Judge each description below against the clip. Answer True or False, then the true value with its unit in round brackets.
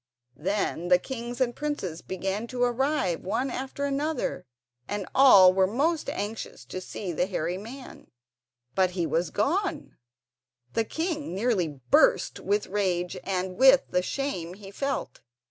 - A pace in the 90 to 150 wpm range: True (145 wpm)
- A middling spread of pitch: False (6.5 semitones)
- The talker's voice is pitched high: True (205 Hz)